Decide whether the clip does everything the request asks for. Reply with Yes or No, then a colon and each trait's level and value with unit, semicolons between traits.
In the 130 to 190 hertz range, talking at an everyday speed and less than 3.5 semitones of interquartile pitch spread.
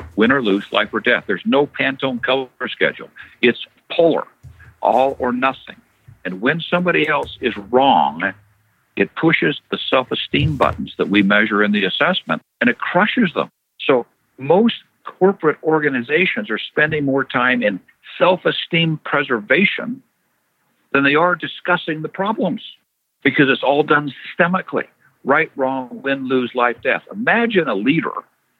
No: medium, 140 Hz; average, 145 wpm; wide, 5.6 semitones